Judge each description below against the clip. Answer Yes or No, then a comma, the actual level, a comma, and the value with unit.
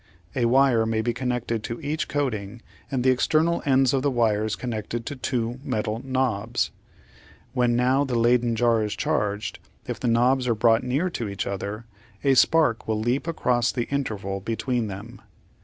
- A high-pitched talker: No, low, 120 Hz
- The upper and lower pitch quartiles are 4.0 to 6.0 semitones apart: No, average, 2.8 semitones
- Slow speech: No, average, 175 wpm